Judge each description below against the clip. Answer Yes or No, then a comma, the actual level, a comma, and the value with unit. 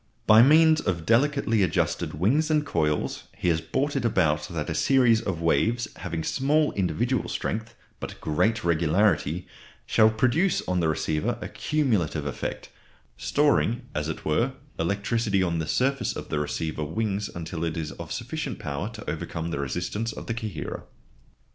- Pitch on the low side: Yes, low, 100 Hz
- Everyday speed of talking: Yes, average, 160 wpm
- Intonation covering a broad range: Yes, wide, 6.7 semitones